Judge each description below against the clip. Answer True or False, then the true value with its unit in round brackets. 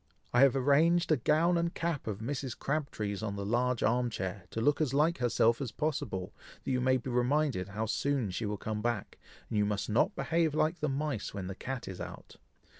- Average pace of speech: False (215 wpm)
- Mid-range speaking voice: False (125 Hz)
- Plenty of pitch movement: True (5.7 semitones)